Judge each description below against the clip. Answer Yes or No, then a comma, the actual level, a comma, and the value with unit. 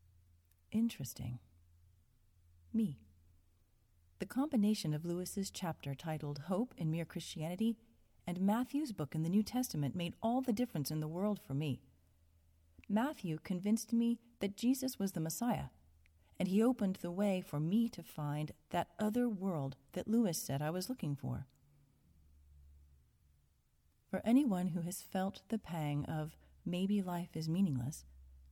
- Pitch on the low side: No, medium, 160 Hz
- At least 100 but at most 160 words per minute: Yes, average, 140 wpm